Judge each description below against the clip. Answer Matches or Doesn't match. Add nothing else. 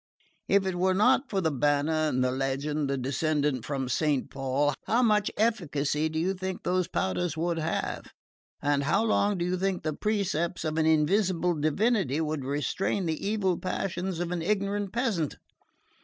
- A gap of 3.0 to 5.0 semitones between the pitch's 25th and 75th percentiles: Matches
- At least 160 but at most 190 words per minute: Matches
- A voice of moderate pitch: Matches